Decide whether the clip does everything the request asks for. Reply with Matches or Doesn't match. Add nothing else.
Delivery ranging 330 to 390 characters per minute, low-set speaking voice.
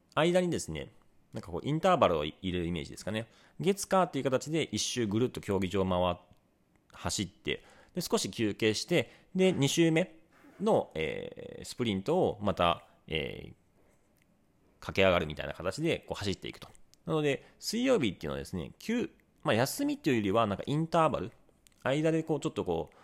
Matches